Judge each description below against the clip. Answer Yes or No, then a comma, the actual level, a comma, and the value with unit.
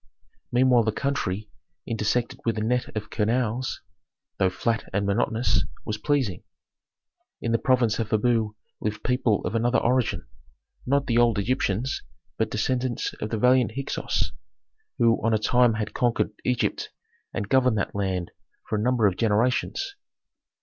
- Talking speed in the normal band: Yes, average, 150 wpm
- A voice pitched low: Yes, low, 115 Hz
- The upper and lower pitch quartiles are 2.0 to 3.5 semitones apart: Yes, average, 2.8 semitones